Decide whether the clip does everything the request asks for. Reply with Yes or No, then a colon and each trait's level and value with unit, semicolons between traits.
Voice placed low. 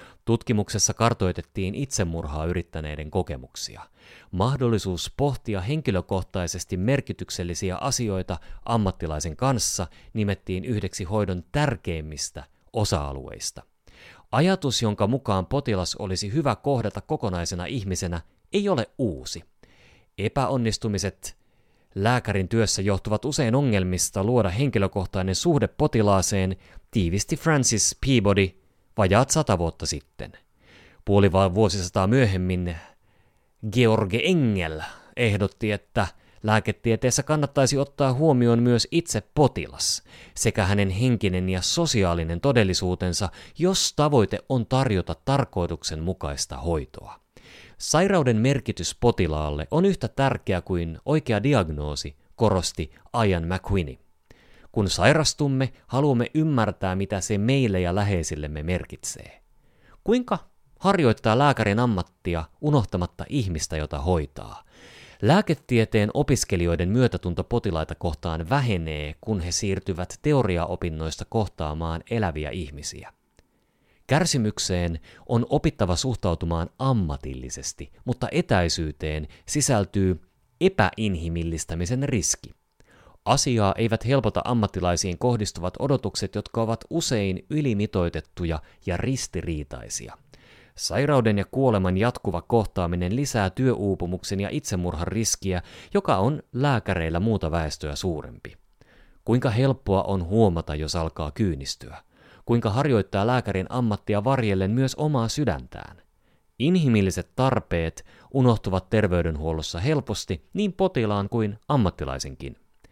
Yes: low, 100 Hz